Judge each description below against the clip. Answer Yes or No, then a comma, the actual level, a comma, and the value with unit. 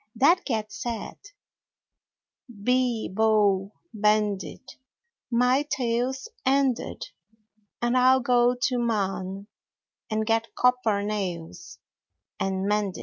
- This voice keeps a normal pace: No, slow, 100 wpm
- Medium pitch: No, high, 225 Hz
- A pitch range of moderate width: Yes, average, 3.7 semitones